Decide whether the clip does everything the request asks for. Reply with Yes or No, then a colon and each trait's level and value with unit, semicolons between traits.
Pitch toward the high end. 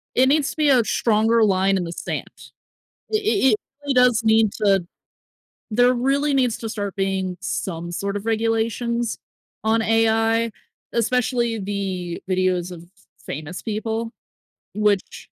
Yes: high, 220 Hz